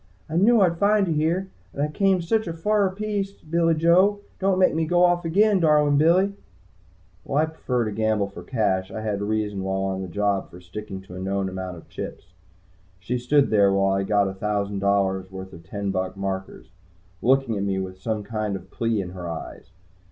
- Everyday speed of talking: No, fast, 210 wpm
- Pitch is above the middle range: No, low, 110 Hz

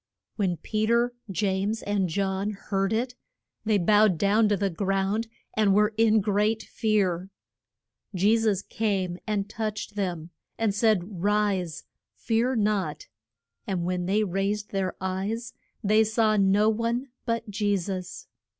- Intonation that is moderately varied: No, narrow, 2.2 semitones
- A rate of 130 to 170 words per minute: Yes, average, 140 wpm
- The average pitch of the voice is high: Yes, high, 205 Hz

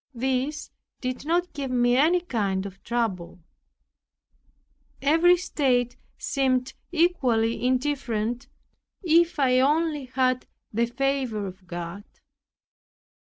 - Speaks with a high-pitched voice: Yes, very high, 255 Hz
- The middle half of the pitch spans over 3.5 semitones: Yes, average, 4.1 semitones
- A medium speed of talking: No, slow, 100 wpm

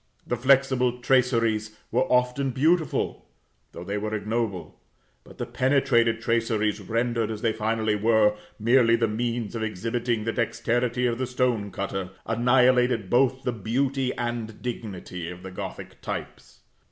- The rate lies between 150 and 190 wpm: No, average, 140 wpm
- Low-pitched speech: Yes, low, 115 Hz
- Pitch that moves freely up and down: No, narrow, 2.5 semitones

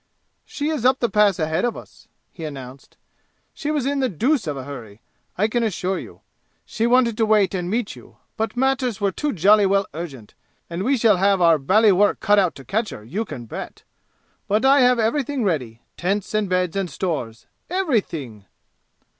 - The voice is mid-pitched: No, high, 200 Hz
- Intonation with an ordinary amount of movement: No, wide, 6.5 semitones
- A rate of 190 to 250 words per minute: Yes, average, 195 wpm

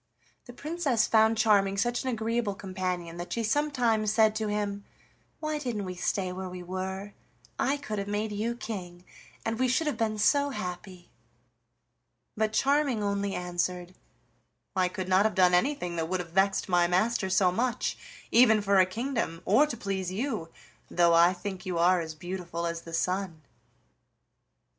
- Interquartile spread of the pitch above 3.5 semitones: Yes, average, 3.9 semitones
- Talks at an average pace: Yes, average, 170 wpm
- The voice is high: Yes, high, 200 Hz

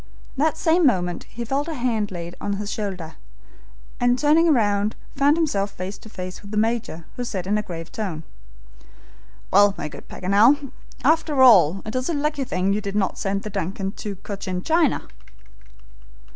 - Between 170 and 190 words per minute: Yes, average, 175 wpm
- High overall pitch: Yes, high, 210 Hz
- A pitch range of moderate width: No, wide, 5.7 semitones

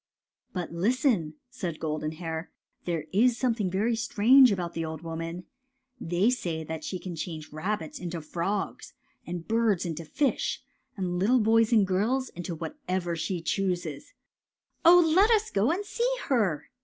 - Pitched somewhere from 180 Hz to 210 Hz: Yes, medium, 185 Hz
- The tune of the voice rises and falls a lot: Yes, wide, 5.8 semitones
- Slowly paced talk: No, average, 160 wpm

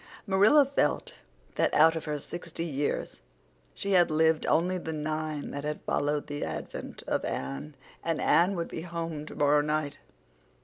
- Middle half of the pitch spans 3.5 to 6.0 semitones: No, average, 2.7 semitones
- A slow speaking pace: No, average, 160 wpm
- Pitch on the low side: No, medium, 155 Hz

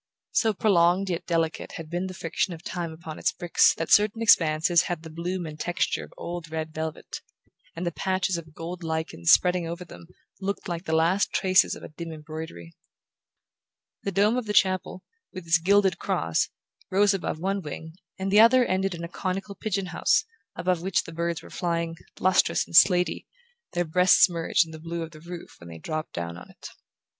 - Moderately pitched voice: Yes, medium, 170 Hz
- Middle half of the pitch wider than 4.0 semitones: No, narrow, 2.6 semitones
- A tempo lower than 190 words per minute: No, average, 195 wpm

